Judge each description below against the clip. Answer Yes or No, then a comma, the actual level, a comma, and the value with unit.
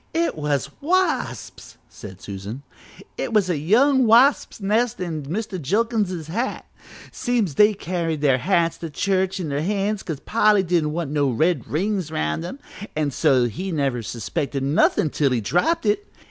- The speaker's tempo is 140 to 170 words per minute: Yes, average, 160 wpm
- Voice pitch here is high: No, medium, 175 Hz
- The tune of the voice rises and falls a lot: Yes, wide, 6.5 semitones